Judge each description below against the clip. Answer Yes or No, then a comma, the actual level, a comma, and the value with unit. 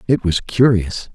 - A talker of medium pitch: No, low, 105 Hz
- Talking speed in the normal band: Yes, average, 155 wpm